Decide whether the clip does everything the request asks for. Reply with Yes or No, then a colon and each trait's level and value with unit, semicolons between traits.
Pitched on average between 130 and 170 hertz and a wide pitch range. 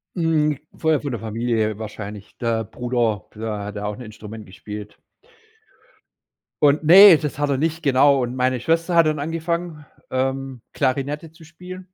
Yes: low, 135 Hz; wide, 6.0 semitones